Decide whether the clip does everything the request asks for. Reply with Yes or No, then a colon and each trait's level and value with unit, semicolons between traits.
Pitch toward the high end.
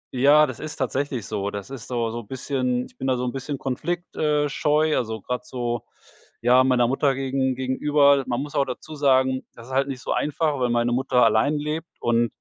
No: low, 130 Hz